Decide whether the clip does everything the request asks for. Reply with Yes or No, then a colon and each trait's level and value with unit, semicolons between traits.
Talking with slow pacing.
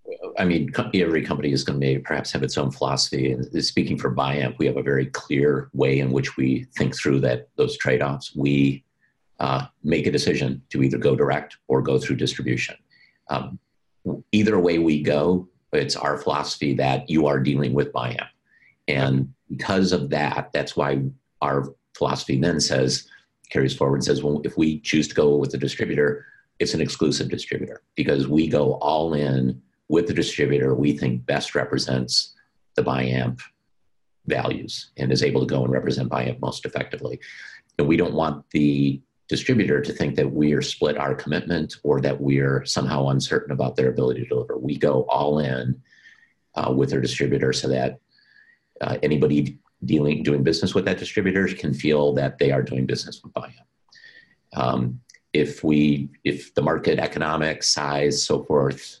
No: average, 175 wpm